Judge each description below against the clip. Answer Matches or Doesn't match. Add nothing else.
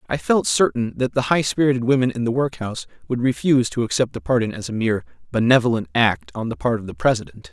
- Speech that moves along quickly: Matches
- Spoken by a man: Matches